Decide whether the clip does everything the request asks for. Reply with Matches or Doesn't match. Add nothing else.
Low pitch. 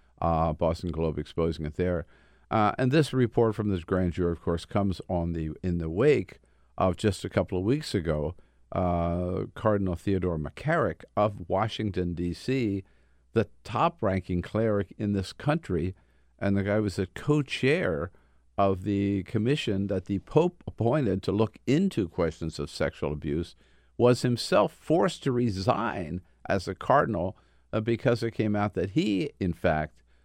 Matches